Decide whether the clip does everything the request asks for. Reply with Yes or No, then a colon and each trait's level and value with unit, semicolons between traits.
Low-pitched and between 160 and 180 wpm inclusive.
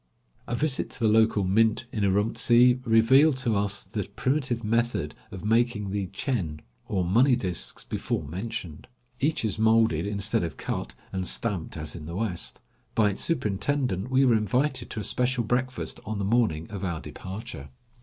Yes: low, 110 Hz; average, 170 wpm